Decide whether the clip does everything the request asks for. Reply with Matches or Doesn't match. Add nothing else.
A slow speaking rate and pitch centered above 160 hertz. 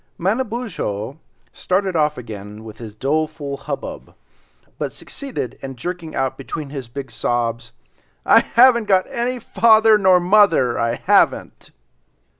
Doesn't match